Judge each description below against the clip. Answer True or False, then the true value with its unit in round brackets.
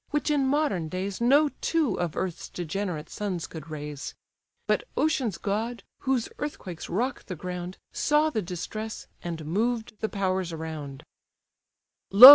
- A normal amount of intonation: False (6.3 semitones)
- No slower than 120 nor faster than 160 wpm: True (140 wpm)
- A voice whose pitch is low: False (195 Hz)